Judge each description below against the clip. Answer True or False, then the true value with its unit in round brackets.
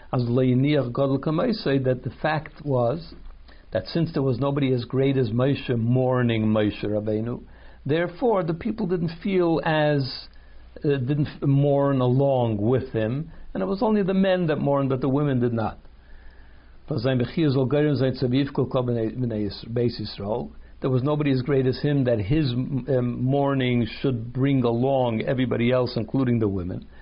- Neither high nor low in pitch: False (130 Hz)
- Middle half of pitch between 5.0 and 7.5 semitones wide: False (3.5 semitones)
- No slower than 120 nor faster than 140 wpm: True (135 wpm)